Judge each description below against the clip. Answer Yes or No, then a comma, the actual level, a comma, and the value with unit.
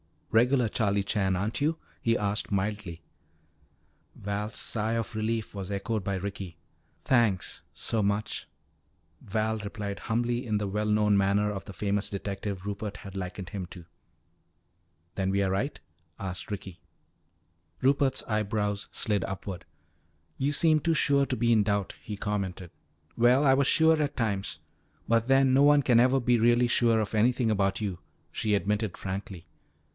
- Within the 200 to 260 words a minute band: No, average, 155 wpm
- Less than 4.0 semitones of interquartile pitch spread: Yes, average, 3.2 semitones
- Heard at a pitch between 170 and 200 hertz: No, low, 105 Hz